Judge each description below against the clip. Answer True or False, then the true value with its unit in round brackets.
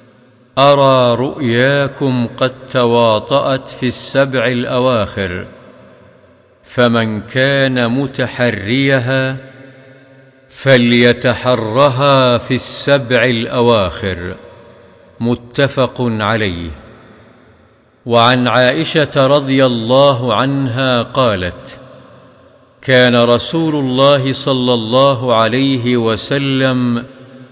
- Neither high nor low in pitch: False (125 Hz)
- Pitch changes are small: True (2.0 semitones)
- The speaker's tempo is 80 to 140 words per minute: False (65 wpm)